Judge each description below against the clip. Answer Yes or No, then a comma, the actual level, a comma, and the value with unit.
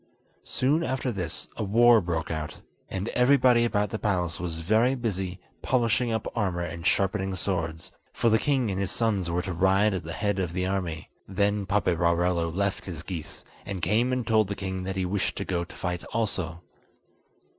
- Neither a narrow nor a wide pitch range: Yes, average, 4.0 semitones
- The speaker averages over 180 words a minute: Yes, average, 190 wpm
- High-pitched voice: No, very low, 95 Hz